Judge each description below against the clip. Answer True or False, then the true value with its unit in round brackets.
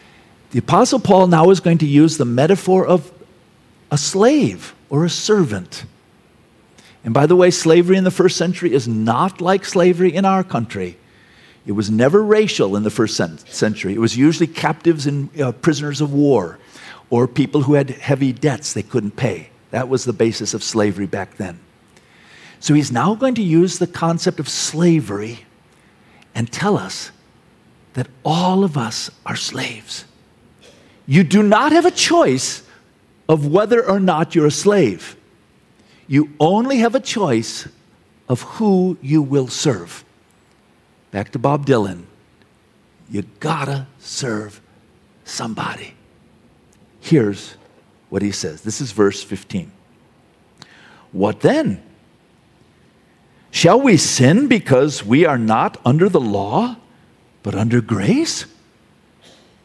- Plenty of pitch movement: True (7.8 semitones)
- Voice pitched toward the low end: False (145 Hz)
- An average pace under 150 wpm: True (140 wpm)